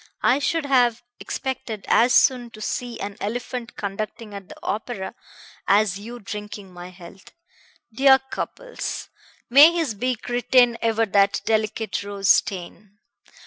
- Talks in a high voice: Yes, high, 225 Hz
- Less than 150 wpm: Yes, slow, 135 wpm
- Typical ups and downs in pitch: Yes, average, 3.6 semitones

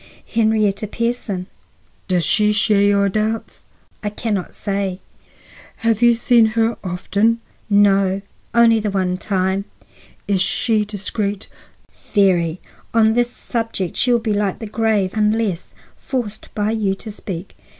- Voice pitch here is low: No, high, 210 Hz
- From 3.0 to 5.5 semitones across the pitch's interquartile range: No, narrow, 2.4 semitones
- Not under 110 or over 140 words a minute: Yes, slow, 135 wpm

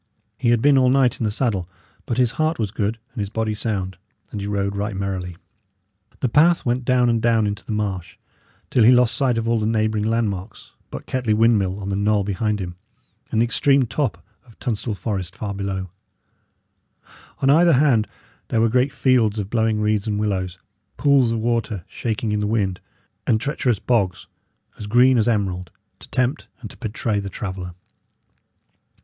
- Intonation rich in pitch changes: No, average, 3.3 semitones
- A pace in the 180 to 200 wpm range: Yes, average, 185 wpm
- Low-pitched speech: Yes, low, 110 Hz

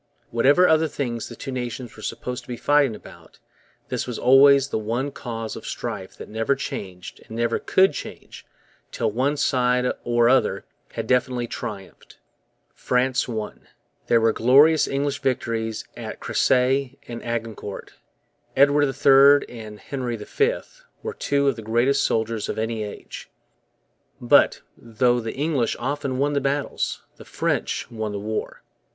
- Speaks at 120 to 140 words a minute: No, average, 150 wpm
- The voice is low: Yes, low, 125 Hz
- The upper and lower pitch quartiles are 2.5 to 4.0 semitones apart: Yes, average, 3.5 semitones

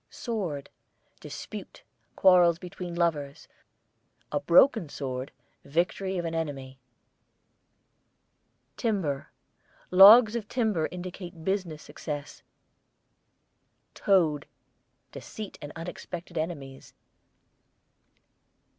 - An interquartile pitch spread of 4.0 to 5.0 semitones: Yes, average, 4.4 semitones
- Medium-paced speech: No, slow, 75 wpm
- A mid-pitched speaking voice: Yes, medium, 170 Hz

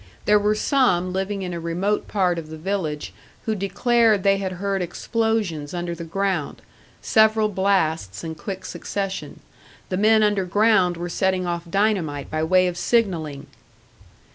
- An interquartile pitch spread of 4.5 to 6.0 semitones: No, average, 3.4 semitones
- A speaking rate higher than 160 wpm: No, average, 150 wpm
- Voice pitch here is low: No, high, 190 Hz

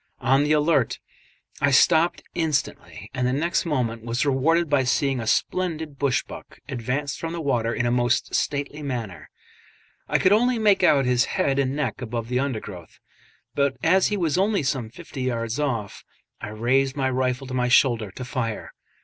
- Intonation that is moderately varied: Yes, average, 3.6 semitones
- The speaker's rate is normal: Yes, average, 180 wpm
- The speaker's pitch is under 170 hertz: Yes, low, 135 Hz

